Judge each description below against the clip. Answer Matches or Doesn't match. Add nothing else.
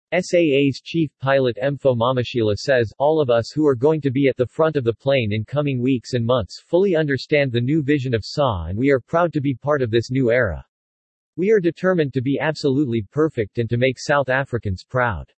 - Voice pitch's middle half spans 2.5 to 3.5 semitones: Doesn't match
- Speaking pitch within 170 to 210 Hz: Doesn't match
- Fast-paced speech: Matches